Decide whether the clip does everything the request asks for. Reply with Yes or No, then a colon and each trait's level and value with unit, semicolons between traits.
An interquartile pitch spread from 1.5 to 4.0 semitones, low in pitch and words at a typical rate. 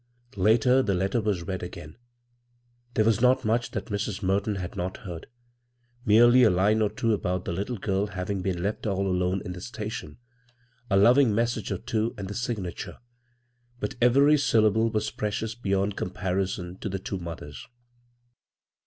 Yes: average, 3.5 semitones; low, 105 Hz; average, 170 wpm